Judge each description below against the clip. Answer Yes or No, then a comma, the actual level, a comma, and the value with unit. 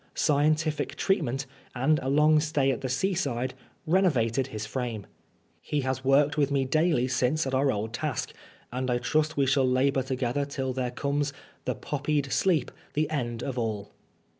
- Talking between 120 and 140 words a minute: No, average, 170 wpm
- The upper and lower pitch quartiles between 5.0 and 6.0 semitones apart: No, average, 3.1 semitones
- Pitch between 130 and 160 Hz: Yes, low, 135 Hz